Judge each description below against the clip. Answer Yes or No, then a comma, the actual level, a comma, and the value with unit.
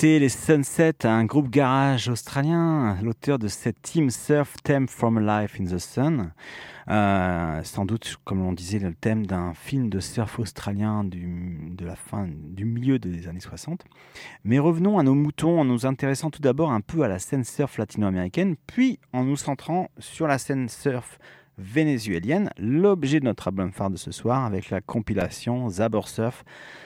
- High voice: No, low, 115 Hz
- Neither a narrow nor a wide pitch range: No, wide, 6.2 semitones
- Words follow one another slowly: No, average, 175 wpm